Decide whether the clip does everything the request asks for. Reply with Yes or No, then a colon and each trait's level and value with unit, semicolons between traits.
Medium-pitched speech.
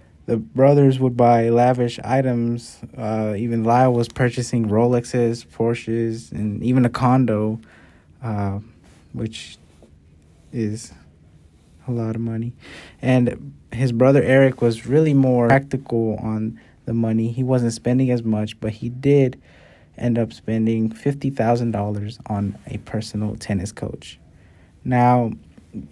No: low, 115 Hz